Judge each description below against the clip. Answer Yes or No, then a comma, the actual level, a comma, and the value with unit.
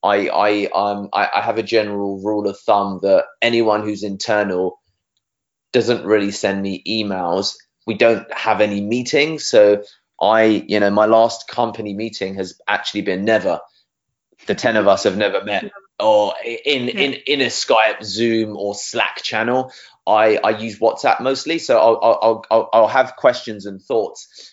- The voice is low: Yes, low, 110 Hz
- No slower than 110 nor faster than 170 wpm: Yes, average, 165 wpm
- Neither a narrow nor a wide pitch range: No, narrow, 2.3 semitones